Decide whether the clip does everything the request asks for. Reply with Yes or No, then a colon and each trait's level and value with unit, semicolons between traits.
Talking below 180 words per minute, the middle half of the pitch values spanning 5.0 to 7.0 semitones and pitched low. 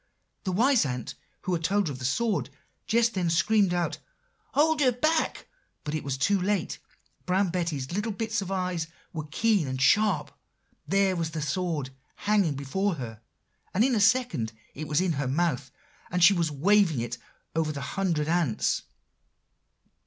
No: average, 170 wpm; wide, 5.5 semitones; medium, 175 Hz